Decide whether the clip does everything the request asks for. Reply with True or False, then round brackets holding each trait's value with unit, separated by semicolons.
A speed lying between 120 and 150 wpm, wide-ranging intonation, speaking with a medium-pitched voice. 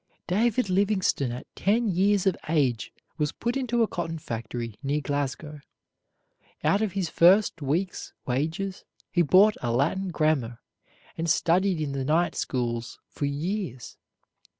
True (140 wpm; 5.8 semitones; 165 Hz)